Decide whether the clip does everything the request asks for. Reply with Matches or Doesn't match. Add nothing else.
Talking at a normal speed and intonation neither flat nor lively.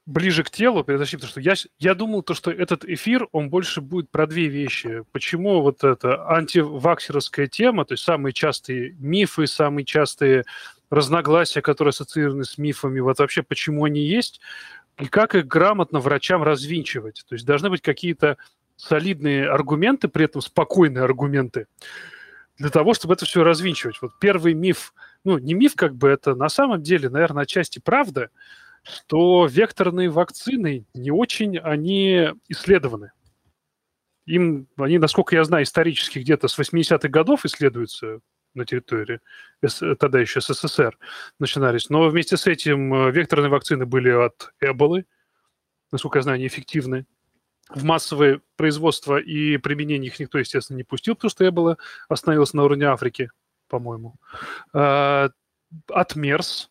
Matches